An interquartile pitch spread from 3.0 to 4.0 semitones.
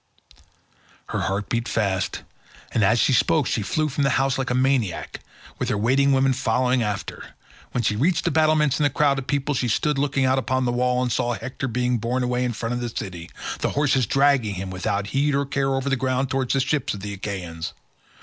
Yes: average, 3.5 semitones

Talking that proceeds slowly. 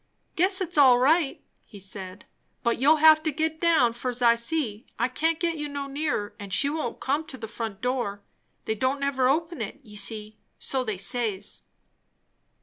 No: average, 185 wpm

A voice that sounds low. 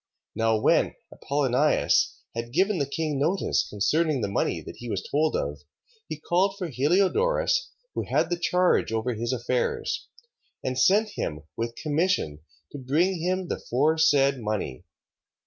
No: medium, 145 Hz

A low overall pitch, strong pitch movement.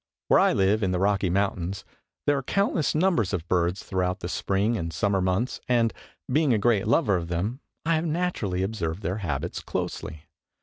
No: low, 100 Hz; average, 4.8 semitones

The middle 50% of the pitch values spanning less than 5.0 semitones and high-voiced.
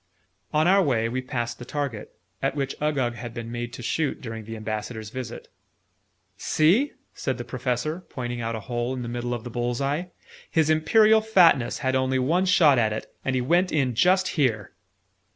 No: average, 4.5 semitones; low, 130 Hz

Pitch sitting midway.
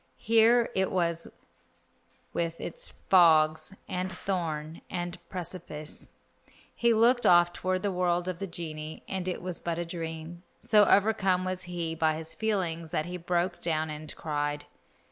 Yes: medium, 175 Hz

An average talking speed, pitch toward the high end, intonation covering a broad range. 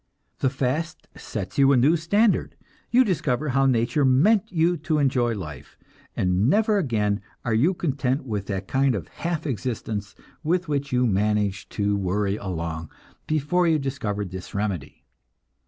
No: average, 155 wpm; low, 130 Hz; wide, 7.1 semitones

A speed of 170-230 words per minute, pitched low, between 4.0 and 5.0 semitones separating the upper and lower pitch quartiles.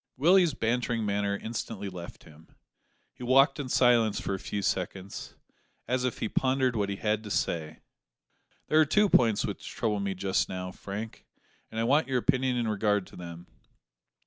Yes: average, 175 wpm; low, 110 Hz; average, 4.4 semitones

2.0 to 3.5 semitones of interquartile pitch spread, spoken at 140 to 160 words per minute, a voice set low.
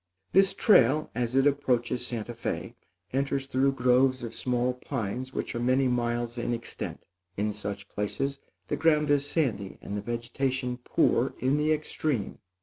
Yes: narrow, 2.6 semitones; average, 155 wpm; low, 125 Hz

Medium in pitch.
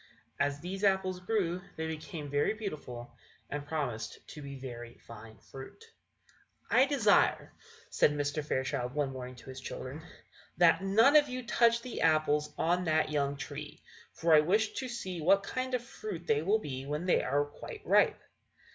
Yes: medium, 155 Hz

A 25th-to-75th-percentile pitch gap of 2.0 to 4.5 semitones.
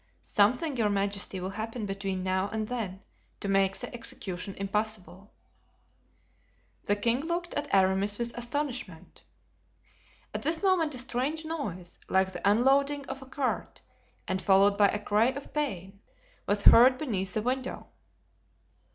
No: average, 5.3 semitones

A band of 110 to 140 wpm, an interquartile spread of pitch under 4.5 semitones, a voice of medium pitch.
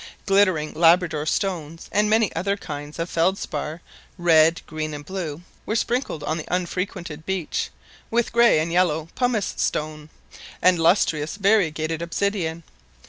Yes: slow, 135 wpm; average, 3.9 semitones; medium, 170 Hz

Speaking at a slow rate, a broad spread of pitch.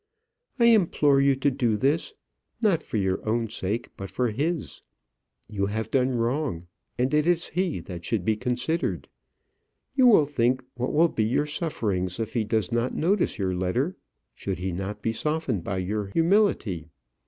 No: average, 170 wpm; wide, 6.9 semitones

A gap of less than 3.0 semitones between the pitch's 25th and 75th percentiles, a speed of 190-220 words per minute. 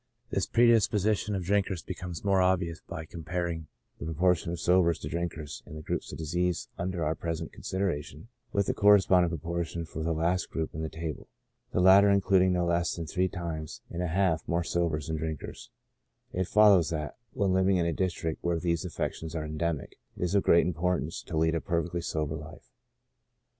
Yes: narrow, 2.4 semitones; average, 195 wpm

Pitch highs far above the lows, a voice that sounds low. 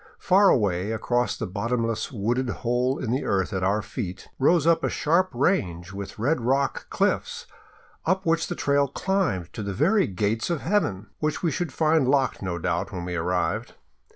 Yes: wide, 8.2 semitones; low, 125 Hz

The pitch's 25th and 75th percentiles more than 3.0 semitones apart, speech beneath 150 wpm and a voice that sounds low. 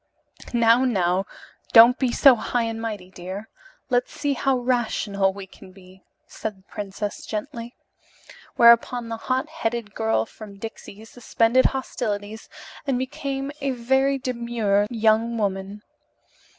No: average, 3.6 semitones; slow, 135 wpm; high, 225 Hz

